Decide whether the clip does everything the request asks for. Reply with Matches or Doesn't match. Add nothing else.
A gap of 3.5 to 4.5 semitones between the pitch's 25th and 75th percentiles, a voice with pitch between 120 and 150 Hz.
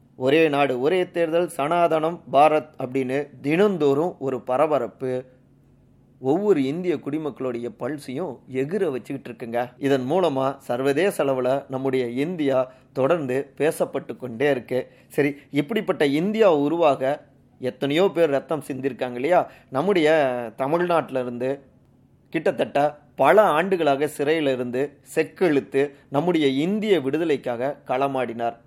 Doesn't match